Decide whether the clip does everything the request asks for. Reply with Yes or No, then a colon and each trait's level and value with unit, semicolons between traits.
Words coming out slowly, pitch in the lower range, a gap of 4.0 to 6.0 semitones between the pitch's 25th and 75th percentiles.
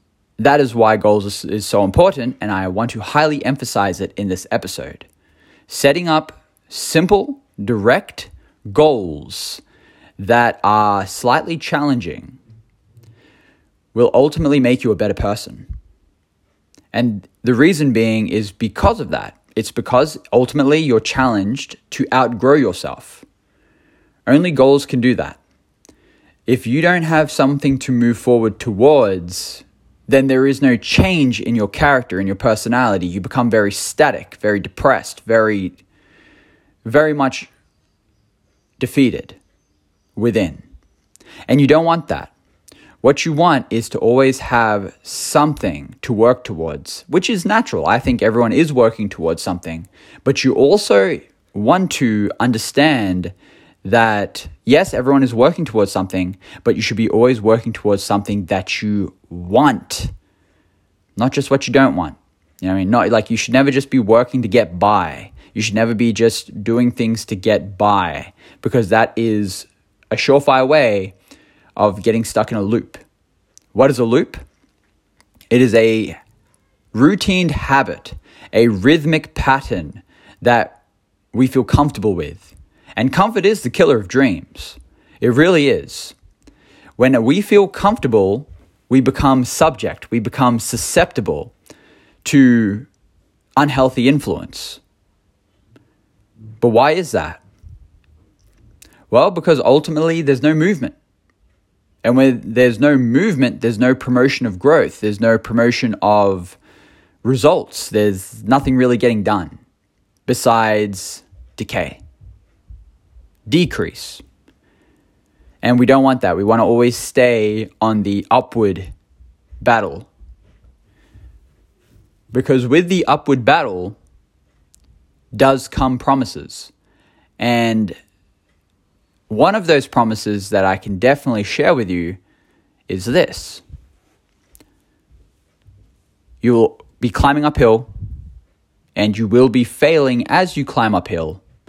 Yes: slow, 130 wpm; low, 110 Hz; average, 5.0 semitones